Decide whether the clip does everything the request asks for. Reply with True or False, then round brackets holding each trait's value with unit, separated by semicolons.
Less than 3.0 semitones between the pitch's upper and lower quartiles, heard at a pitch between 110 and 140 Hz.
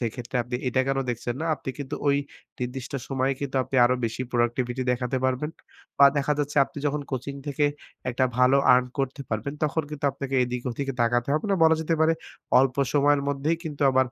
True (2.4 semitones; 135 Hz)